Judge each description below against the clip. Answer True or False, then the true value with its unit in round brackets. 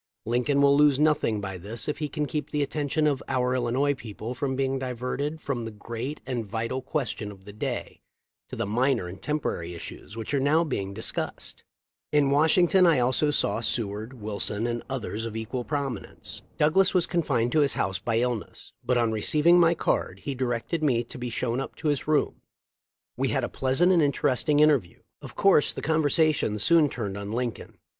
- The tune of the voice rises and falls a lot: False (4.7 semitones)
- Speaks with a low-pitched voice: True (130 Hz)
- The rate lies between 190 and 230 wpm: True (205 wpm)